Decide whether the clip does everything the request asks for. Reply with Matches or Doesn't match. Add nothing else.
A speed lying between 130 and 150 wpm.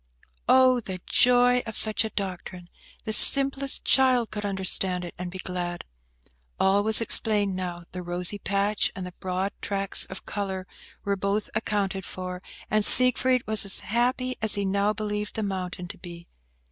Doesn't match